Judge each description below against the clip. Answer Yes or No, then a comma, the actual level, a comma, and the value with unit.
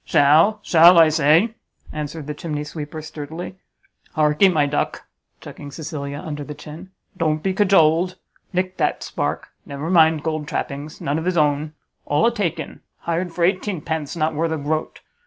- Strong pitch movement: No, narrow, 2.5 semitones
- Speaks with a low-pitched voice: No, medium, 155 Hz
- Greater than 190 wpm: No, average, 160 wpm